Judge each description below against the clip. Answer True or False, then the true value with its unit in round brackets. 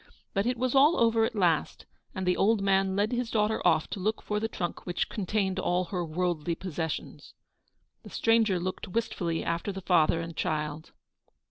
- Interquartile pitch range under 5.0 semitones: True (4.1 semitones)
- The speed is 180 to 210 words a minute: True (185 wpm)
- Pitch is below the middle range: False (190 Hz)